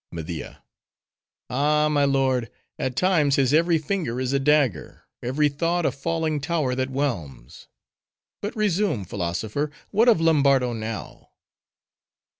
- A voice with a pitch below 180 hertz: Yes, medium, 140 Hz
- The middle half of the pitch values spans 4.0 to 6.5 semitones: Yes, average, 4.5 semitones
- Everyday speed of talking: No, slow, 115 wpm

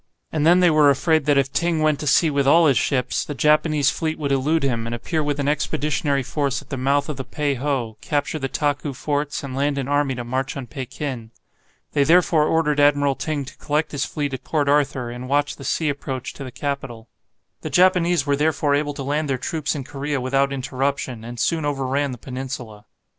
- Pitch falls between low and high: Yes, medium, 145 Hz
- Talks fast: Yes, fast, 215 wpm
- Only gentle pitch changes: Yes, narrow, 2.0 semitones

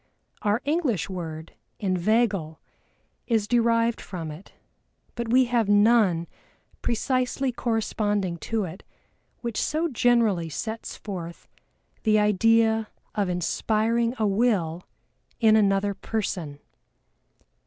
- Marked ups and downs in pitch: No, average, 4.0 semitones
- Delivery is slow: Yes, slow, 100 wpm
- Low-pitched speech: No, high, 215 Hz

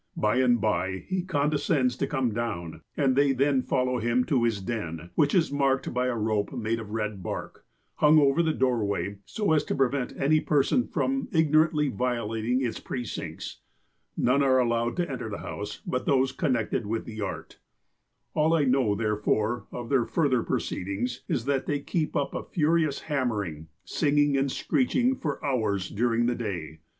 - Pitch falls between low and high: No, low, 125 Hz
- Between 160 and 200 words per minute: Yes, average, 175 wpm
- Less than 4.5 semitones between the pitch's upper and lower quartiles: No, average, 4.8 semitones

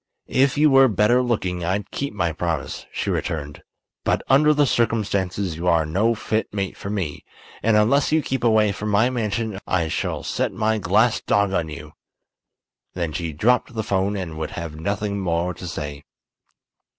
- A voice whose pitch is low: Yes, low, 100 Hz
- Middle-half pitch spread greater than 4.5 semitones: Yes, average, 5.1 semitones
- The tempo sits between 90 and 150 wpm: No, average, 175 wpm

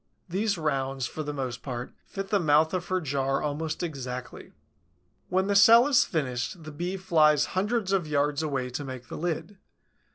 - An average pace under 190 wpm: Yes, average, 175 wpm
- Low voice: No, medium, 155 Hz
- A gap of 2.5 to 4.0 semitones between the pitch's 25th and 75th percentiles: No, wide, 5.4 semitones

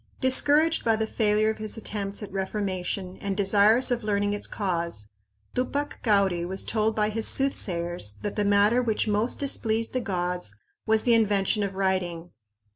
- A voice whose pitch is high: Yes, high, 205 Hz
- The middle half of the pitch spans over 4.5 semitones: No, average, 2.8 semitones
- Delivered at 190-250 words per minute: No, average, 165 wpm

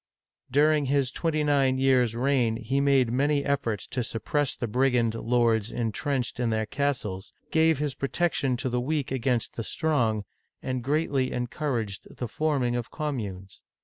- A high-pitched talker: No, low, 130 Hz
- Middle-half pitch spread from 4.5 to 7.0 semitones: No, average, 3.5 semitones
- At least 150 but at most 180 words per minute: Yes, average, 160 wpm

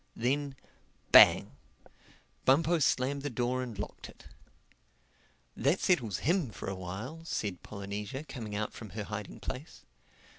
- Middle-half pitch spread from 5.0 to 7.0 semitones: Yes, wide, 5.5 semitones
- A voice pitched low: Yes, low, 125 Hz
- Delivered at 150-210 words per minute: No, slow, 135 wpm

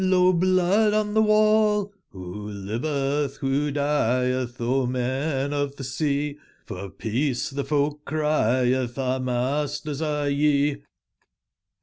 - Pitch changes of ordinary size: Yes, average, 3.1 semitones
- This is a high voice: No, medium, 140 Hz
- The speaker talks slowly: Yes, slow, 115 wpm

